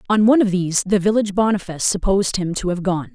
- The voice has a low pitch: No, high, 195 Hz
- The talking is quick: Yes, fast, 230 wpm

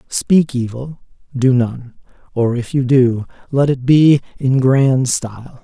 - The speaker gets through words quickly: No, average, 150 wpm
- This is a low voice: Yes, low, 130 Hz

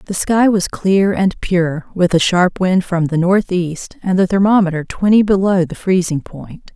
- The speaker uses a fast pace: No, average, 185 wpm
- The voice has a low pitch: No, medium, 185 Hz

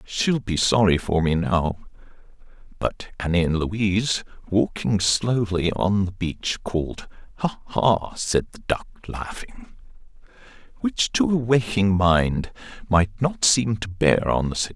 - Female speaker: No, male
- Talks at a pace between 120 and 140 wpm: Yes, slow, 135 wpm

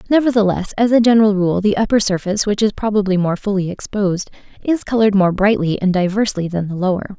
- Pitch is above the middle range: Yes, high, 200 Hz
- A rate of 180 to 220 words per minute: Yes, average, 190 wpm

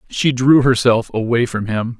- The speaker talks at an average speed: Yes, average, 180 wpm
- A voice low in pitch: Yes, low, 120 Hz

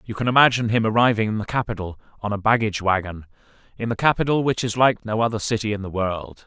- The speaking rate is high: Yes, fast, 215 wpm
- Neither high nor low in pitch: No, low, 110 Hz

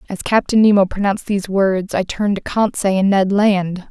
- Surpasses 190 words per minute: Yes, average, 200 wpm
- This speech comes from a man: No, female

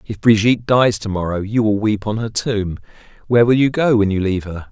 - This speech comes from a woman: No, male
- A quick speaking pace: Yes, fast, 240 wpm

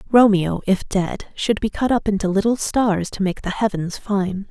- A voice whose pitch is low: No, high, 200 Hz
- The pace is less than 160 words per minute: No, average, 200 wpm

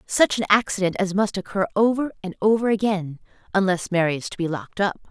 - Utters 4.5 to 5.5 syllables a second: No, 6.1 syllables/s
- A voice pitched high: Yes, high, 195 Hz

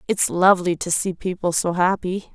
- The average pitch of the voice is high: No, medium, 180 Hz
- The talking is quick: No, average, 180 wpm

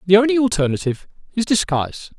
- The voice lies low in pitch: No, high, 190 Hz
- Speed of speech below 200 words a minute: Yes, average, 140 wpm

